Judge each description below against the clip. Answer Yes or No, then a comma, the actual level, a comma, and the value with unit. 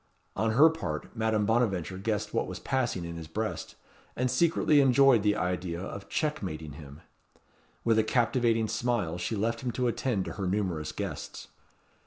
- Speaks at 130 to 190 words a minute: Yes, average, 165 wpm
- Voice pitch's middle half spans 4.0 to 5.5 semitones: Yes, average, 5.0 semitones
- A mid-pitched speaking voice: No, low, 110 Hz